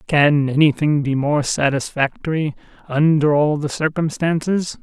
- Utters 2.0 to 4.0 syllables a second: No, 4.4 syllables/s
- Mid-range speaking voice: Yes, medium, 150 Hz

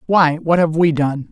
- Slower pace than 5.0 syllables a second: Yes, 4.5 syllables/s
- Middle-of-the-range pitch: Yes, medium, 160 Hz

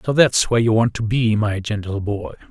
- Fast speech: Yes, fast, 240 wpm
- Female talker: No, male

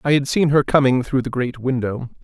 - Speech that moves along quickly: Yes, fast, 240 wpm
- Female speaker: No, male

